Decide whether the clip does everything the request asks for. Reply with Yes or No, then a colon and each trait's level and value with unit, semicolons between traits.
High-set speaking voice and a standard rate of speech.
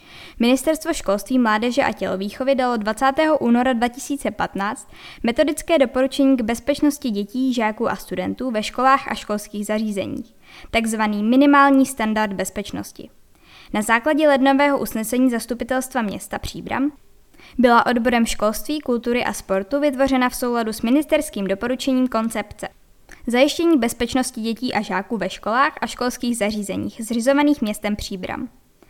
Yes: high, 245 Hz; average, 125 wpm